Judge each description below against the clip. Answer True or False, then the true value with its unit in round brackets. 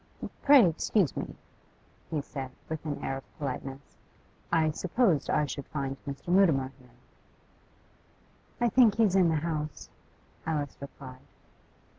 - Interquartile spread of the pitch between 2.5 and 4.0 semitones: False (4.7 semitones)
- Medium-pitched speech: True (150 Hz)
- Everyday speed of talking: False (130 wpm)